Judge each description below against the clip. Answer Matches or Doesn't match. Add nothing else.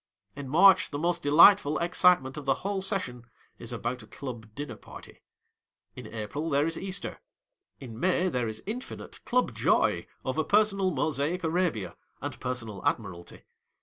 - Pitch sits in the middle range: Matches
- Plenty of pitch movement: Matches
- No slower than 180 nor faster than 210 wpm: Doesn't match